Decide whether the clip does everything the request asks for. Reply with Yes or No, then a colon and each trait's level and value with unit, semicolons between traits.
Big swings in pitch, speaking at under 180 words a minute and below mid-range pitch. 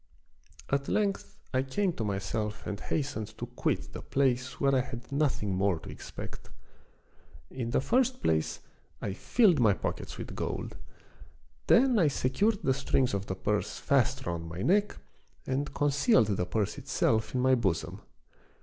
Yes: wide, 5.9 semitones; average, 160 wpm; low, 130 Hz